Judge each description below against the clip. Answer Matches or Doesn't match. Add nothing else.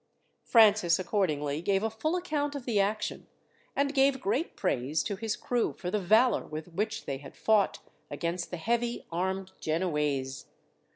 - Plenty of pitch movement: Matches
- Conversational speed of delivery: Matches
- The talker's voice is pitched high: Matches